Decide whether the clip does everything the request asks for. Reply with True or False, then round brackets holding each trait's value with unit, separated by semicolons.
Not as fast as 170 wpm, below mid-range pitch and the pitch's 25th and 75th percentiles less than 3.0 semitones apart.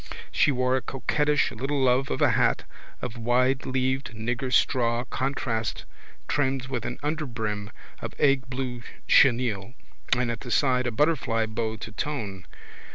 True (150 wpm; 125 Hz; 2.5 semitones)